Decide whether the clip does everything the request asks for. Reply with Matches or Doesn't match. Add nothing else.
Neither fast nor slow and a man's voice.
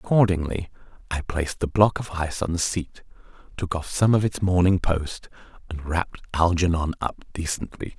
Matches